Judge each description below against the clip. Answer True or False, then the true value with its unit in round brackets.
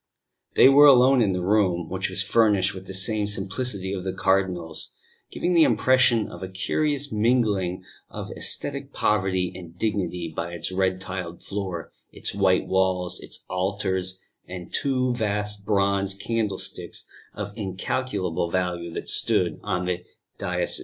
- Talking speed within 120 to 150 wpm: True (145 wpm)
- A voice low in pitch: True (95 Hz)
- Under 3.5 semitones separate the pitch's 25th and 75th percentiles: True (2.8 semitones)